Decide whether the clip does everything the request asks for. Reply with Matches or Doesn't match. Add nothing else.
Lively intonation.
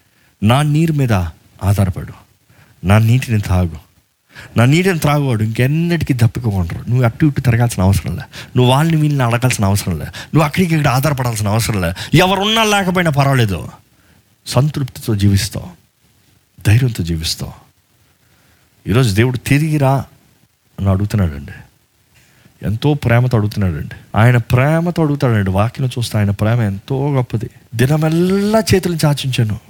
Matches